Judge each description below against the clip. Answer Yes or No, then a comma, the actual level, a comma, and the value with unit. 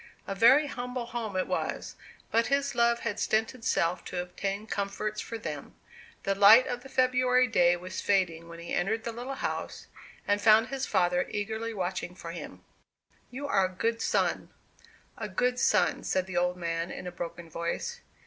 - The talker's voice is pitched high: Yes, high, 210 Hz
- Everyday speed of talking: Yes, average, 180 wpm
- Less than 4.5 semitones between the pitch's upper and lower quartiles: No, average, 5.1 semitones